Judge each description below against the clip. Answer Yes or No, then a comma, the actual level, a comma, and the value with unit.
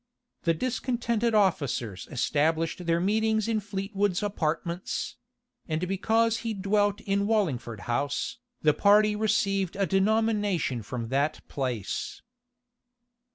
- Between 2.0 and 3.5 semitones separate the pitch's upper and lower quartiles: No, wide, 5.6 semitones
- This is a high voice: Yes, high, 195 Hz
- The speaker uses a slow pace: Yes, slow, 110 wpm